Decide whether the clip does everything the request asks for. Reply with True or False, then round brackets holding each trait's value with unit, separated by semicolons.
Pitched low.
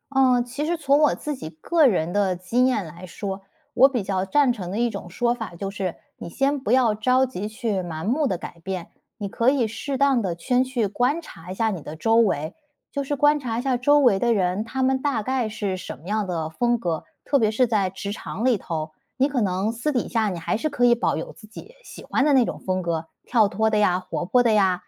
False (225 Hz)